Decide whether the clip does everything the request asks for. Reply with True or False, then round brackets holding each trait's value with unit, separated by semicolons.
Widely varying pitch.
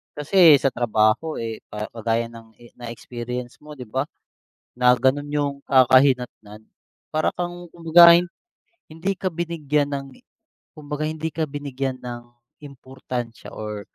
False (4.3 semitones)